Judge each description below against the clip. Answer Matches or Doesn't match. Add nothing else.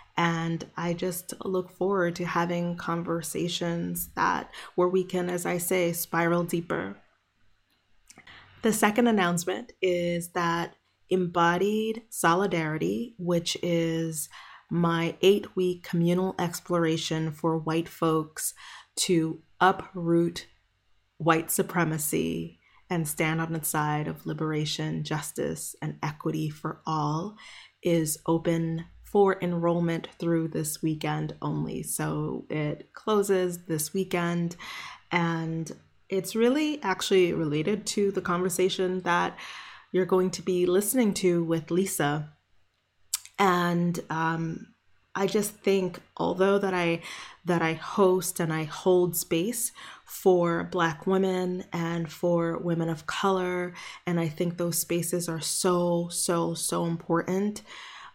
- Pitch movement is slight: Matches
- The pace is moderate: Doesn't match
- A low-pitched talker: Doesn't match